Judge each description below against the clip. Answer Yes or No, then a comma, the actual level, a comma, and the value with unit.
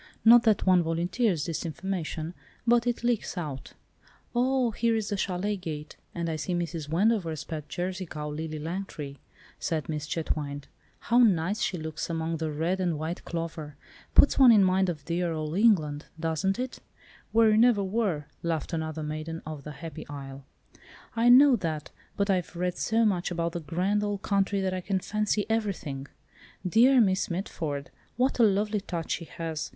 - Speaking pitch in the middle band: Yes, medium, 175 Hz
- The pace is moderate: Yes, average, 175 wpm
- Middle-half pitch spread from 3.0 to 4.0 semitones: No, average, 4.7 semitones